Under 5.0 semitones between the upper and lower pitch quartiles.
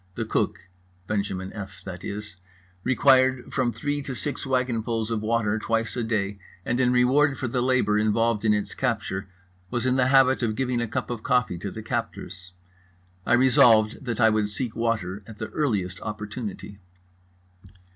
Yes: average, 3.2 semitones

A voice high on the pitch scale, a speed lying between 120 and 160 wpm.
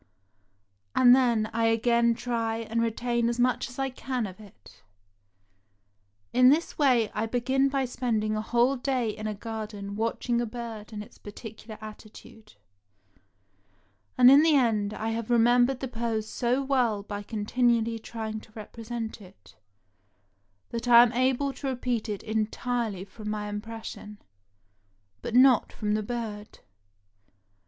Yes: high, 230 Hz; average, 145 wpm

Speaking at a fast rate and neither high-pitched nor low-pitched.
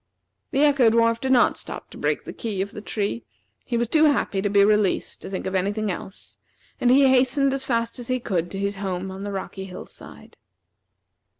No: fast, 220 wpm; high, 215 Hz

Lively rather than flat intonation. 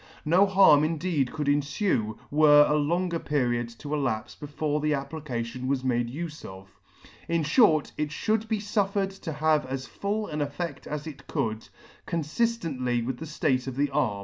No: average, 4.1 semitones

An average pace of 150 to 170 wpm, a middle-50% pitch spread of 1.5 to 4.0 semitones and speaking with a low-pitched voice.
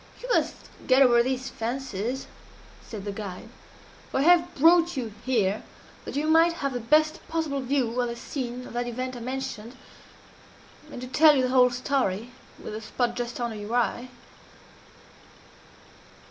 No: average, 165 wpm; average, 2.7 semitones; very high, 250 Hz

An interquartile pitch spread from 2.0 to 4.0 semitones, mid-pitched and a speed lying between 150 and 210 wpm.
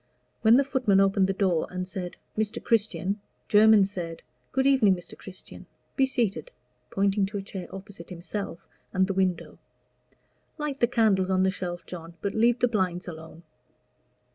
No: average, 3.2 semitones; high, 195 Hz; average, 165 wpm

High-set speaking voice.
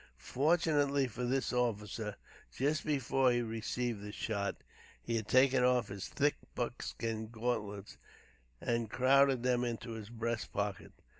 No: low, 120 Hz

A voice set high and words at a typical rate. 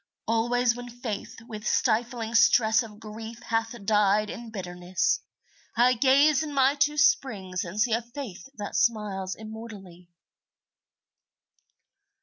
No: high, 225 Hz; slow, 125 wpm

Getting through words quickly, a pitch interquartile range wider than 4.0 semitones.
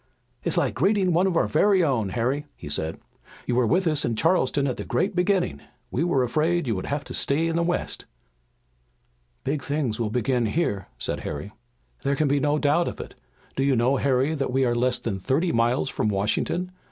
Yes: fast, 215 wpm; wide, 5.6 semitones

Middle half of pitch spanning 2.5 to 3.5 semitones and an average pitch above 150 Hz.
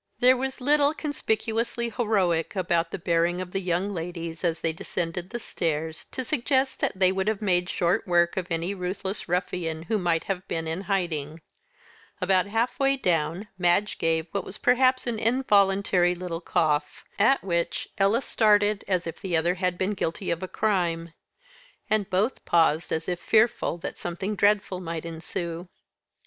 No: average, 3.9 semitones; medium, 185 Hz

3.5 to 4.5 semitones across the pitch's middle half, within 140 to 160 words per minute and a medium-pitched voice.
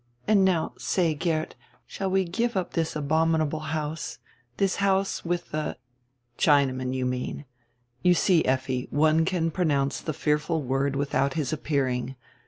Yes: average, 3.9 semitones; average, 155 wpm; medium, 155 Hz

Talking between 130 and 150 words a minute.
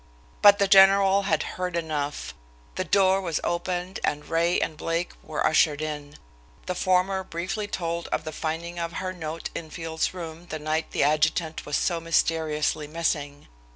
No: average, 165 wpm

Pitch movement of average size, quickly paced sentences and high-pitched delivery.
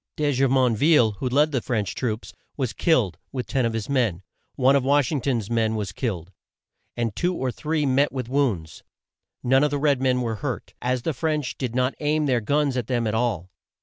No: average, 3.7 semitones; fast, 215 wpm; low, 130 Hz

